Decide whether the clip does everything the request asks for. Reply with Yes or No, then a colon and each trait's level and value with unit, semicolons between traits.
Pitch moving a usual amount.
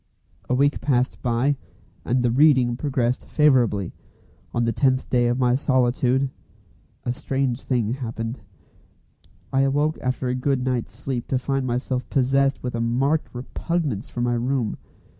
No: narrow, 2.1 semitones